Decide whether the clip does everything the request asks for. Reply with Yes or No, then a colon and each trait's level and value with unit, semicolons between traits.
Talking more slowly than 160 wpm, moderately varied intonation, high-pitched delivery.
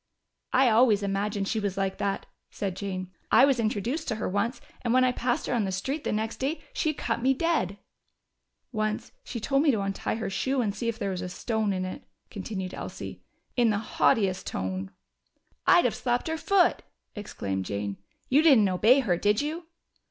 No: average, 195 wpm; average, 4.7 semitones; high, 215 Hz